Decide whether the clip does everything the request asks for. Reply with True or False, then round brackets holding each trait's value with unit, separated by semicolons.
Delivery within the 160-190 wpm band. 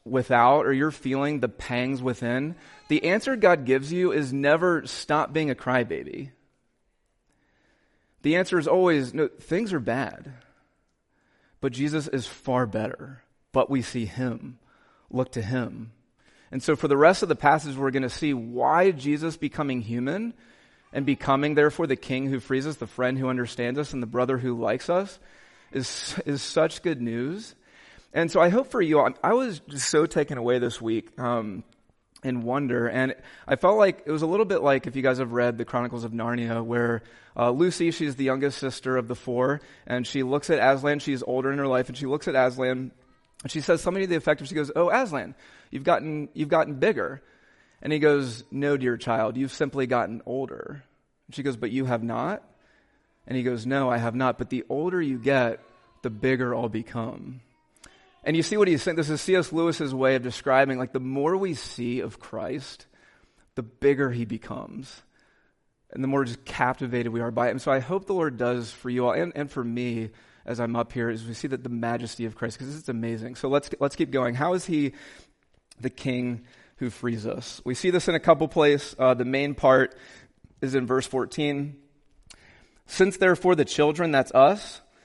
False (200 wpm)